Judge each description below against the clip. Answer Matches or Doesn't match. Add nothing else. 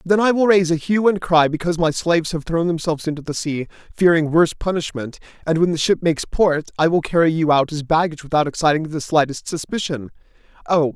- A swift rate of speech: Matches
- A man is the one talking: Matches